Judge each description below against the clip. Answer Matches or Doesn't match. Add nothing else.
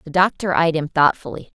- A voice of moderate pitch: Matches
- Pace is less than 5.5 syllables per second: Doesn't match